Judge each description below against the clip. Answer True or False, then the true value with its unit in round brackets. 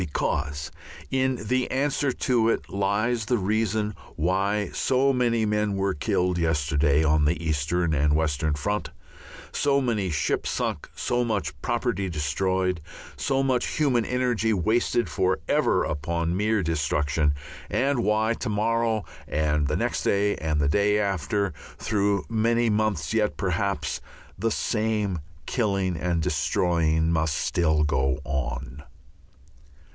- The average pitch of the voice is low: True (100 Hz)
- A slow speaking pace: True (130 wpm)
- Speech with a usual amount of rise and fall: False (6.1 semitones)